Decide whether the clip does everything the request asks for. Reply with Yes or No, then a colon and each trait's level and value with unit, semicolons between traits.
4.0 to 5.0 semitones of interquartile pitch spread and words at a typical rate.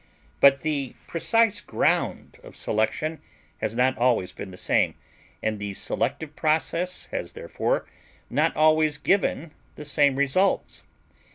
No: average, 4.6 semitones; slow, 125 wpm